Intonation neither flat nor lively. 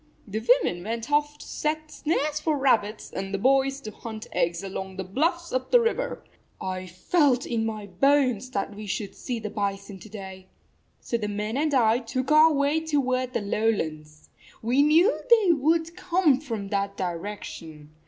No: wide, 6.7 semitones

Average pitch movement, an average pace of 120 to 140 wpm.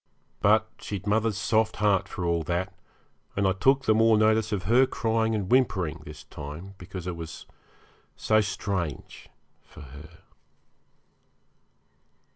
Yes: average, 4.1 semitones; slow, 135 wpm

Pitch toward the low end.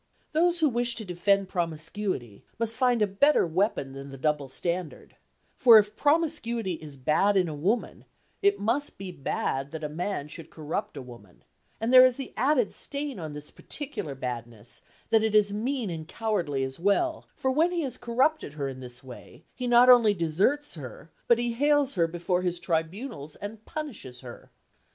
No: high, 200 Hz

